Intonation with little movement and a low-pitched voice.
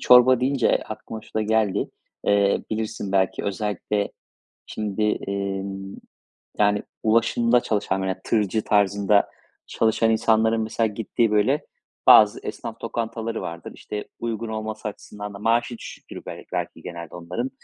Yes: narrow, 2.1 semitones; low, 110 Hz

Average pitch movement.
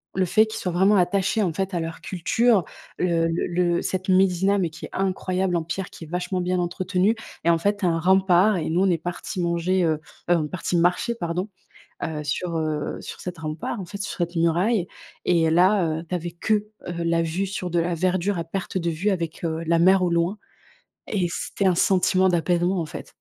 No: narrow, 2.1 semitones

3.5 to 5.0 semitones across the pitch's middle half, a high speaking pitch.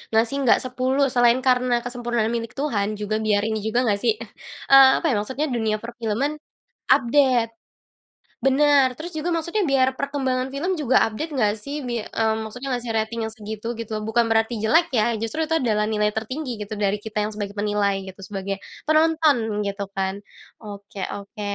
Yes: average, 4.1 semitones; high, 235 Hz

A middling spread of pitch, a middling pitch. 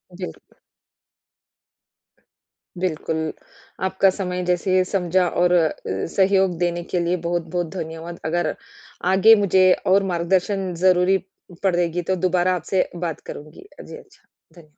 No: narrow, 1.7 semitones; medium, 180 Hz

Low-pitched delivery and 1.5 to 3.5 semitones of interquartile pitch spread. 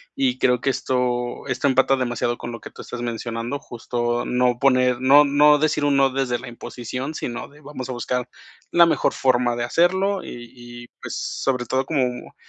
Yes: low, 125 Hz; narrow, 2.6 semitones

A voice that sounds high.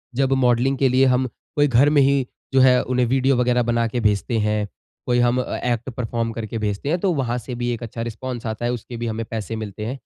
No: low, 120 Hz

